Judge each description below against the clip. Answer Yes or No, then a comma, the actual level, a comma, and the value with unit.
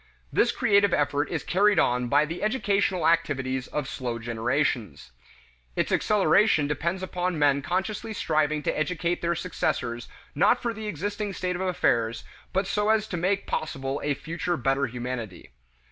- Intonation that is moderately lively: No, wide, 6.1 semitones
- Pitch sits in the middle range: Yes, medium, 160 Hz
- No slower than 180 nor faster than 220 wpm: No, average, 155 wpm